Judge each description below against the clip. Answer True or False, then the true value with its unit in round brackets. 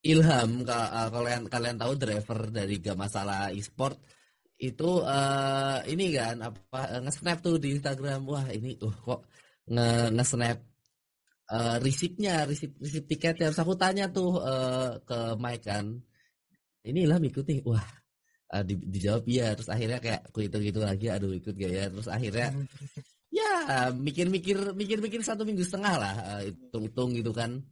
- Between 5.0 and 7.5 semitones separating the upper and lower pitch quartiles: True (5.3 semitones)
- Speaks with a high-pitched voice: False (125 Hz)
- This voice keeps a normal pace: False (145 wpm)